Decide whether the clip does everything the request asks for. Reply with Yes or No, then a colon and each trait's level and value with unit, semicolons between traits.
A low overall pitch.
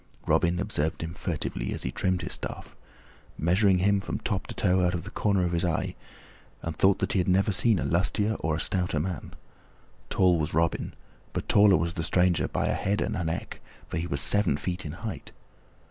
Yes: very low, 90 Hz